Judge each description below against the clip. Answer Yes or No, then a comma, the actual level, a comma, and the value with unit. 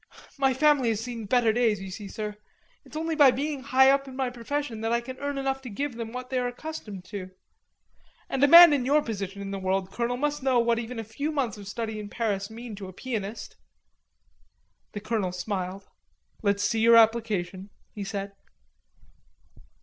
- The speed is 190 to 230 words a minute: Yes, average, 195 wpm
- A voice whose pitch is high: Yes, high, 230 Hz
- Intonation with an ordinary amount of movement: Yes, average, 4.5 semitones